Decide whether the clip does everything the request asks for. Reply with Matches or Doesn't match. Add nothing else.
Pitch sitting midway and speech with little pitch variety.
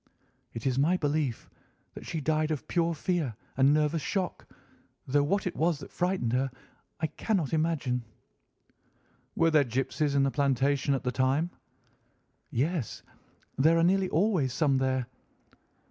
Doesn't match